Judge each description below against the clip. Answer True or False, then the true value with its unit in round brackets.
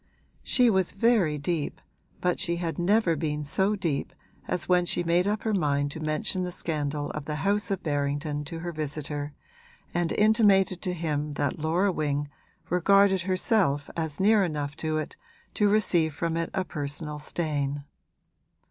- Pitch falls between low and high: True (165 Hz)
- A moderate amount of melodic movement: True (4.2 semitones)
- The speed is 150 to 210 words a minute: True (165 wpm)